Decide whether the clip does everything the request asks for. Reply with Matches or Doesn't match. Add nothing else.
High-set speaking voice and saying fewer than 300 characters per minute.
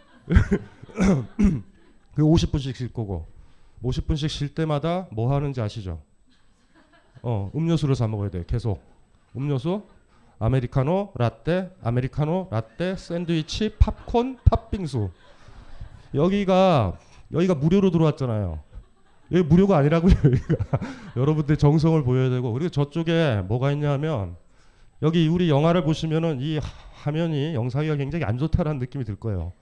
Doesn't match